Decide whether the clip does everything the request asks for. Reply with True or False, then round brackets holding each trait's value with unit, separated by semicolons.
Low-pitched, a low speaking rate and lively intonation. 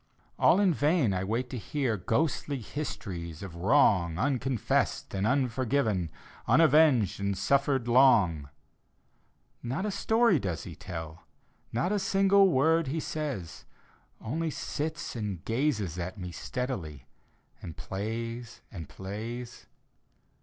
True (120 Hz; 125 wpm; 7.3 semitones)